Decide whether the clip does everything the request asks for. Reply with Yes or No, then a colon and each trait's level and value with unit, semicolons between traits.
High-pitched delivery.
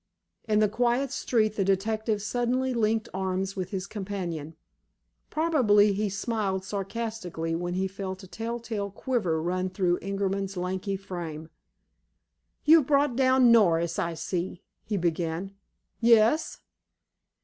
Yes: high, 200 Hz